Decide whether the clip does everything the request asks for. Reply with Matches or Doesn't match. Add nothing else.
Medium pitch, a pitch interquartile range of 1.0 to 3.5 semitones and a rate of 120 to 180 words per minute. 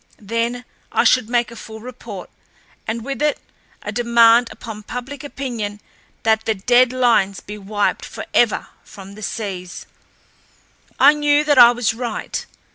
Doesn't match